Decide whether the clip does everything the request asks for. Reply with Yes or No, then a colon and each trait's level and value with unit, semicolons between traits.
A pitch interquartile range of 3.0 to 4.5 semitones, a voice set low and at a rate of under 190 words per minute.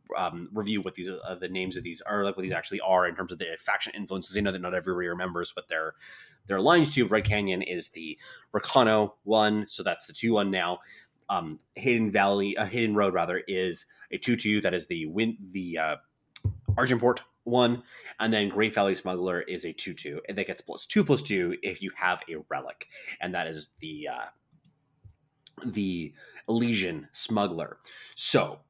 No: average, 3.4 semitones; low, 100 Hz; average, 200 wpm